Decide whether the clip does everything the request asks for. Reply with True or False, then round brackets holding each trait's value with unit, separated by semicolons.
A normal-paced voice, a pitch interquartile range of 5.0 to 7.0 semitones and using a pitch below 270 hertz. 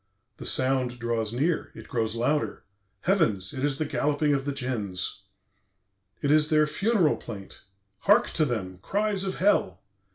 True (155 wpm; 5.4 semitones; 140 Hz)